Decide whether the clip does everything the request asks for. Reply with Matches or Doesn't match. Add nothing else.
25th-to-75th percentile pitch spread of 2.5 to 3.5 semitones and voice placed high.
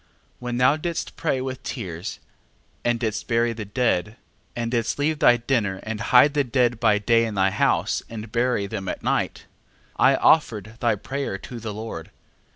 Doesn't match